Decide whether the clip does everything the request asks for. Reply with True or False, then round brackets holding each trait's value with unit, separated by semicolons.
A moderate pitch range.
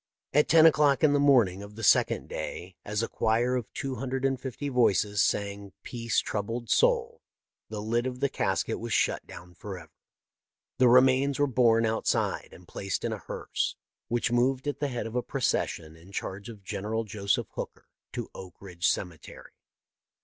True (4.7 semitones)